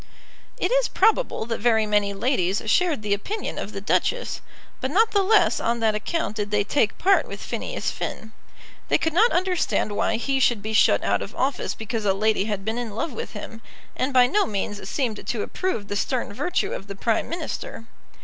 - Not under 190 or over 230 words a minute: Yes, fast, 205 wpm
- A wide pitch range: Yes, wide, 8.0 semitones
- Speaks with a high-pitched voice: Yes, high, 230 Hz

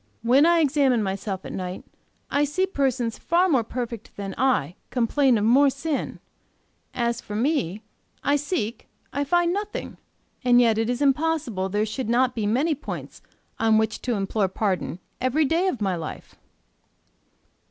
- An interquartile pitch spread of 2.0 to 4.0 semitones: No, average, 5.1 semitones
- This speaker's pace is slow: No, average, 160 wpm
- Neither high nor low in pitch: No, high, 245 Hz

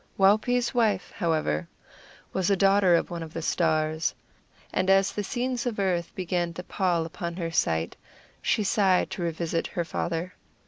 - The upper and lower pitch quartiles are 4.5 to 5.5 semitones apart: No, average, 3.0 semitones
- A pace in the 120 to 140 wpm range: No, average, 165 wpm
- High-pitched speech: No, medium, 180 Hz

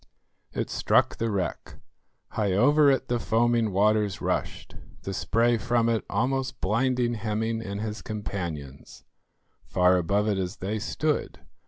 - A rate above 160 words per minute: No, average, 140 wpm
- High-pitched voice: No, low, 110 Hz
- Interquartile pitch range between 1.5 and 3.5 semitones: Yes, average, 3.2 semitones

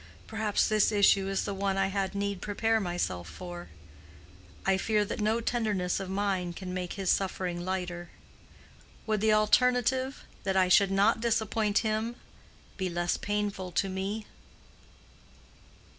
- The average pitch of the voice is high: Yes, high, 200 Hz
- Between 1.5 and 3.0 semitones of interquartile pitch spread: Yes, narrow, 2.5 semitones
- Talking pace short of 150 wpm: Yes, slow, 135 wpm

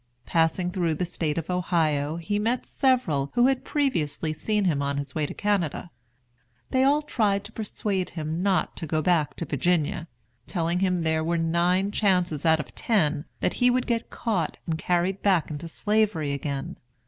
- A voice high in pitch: No, medium, 175 Hz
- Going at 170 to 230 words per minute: Yes, average, 180 wpm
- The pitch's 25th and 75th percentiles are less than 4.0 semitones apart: No, average, 4.6 semitones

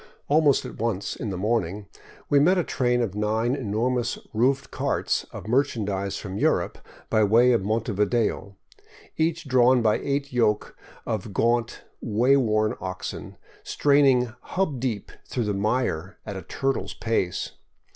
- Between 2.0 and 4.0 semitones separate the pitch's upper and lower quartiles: Yes, average, 3.7 semitones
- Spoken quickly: No, average, 145 wpm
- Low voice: Yes, low, 115 Hz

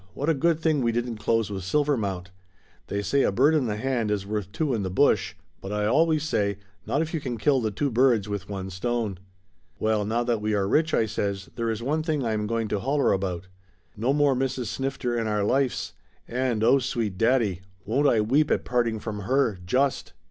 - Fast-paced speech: Yes, fast, 220 wpm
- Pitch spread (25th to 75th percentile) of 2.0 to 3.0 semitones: No, average, 4.6 semitones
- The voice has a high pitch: No, low, 115 Hz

